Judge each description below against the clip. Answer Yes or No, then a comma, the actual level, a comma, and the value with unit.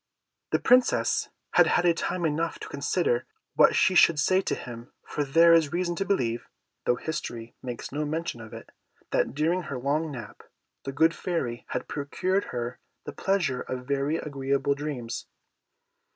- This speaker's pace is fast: No, average, 165 wpm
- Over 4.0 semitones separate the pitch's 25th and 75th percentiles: Yes, average, 4.9 semitones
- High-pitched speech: No, medium, 145 Hz